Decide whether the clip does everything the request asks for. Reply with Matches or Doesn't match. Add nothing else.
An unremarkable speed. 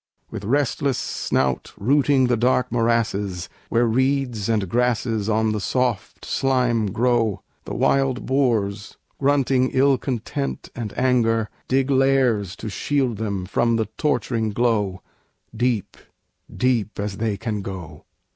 Doesn't match